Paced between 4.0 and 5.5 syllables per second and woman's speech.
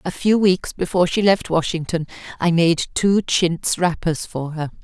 Yes: 4.5 syllables/s; female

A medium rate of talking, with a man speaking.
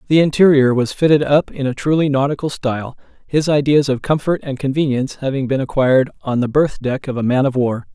No: fast, 210 wpm; male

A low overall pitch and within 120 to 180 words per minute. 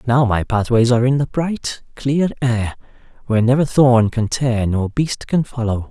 No: low, 125 Hz; average, 195 wpm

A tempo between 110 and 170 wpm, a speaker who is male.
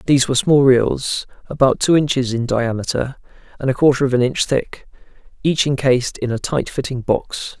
No: average, 180 wpm; male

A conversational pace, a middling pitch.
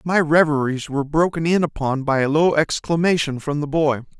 Yes: average, 185 wpm; medium, 150 Hz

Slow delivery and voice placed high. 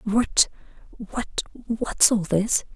Yes: slow, 65 wpm; high, 215 Hz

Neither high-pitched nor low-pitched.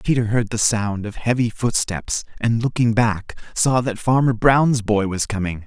No: low, 115 Hz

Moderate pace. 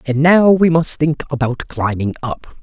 Yes: average, 185 wpm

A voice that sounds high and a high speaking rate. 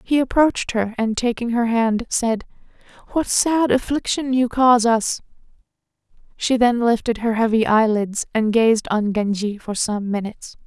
No: high, 230 Hz; average, 150 wpm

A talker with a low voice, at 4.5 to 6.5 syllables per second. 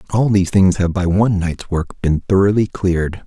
Yes: very low, 95 Hz; 5.3 syllables/s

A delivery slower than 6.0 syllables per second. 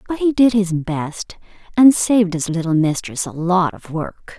Yes: 4.4 syllables/s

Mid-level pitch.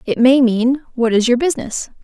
No: very high, 250 Hz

